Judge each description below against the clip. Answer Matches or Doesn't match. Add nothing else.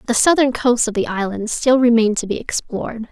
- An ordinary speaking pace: Doesn't match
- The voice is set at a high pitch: Matches